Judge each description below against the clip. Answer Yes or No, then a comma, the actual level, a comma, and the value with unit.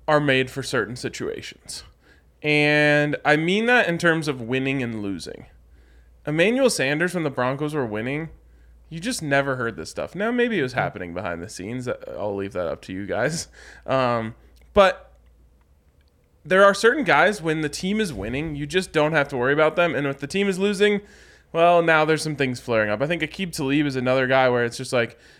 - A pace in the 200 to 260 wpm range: Yes, fast, 205 wpm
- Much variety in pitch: Yes, wide, 6.1 semitones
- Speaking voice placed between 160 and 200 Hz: No, medium, 140 Hz